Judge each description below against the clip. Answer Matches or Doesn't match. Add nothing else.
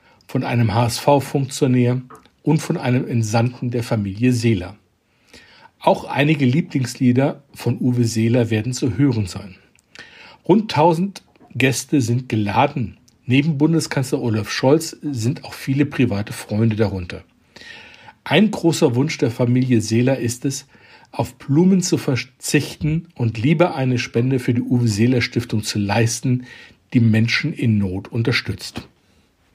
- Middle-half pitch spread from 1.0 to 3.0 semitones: Doesn't match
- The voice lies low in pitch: Matches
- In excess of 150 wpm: Doesn't match